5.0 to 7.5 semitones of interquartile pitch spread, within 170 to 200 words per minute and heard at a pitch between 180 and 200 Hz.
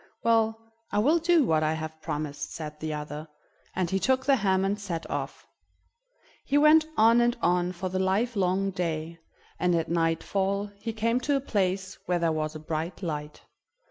Yes: wide, 5.6 semitones; average, 180 wpm; high, 190 Hz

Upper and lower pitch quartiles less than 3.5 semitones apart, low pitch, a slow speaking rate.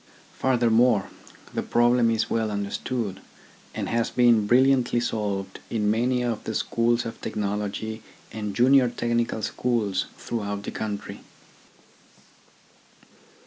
Yes: narrow, 2.5 semitones; low, 115 Hz; slow, 110 wpm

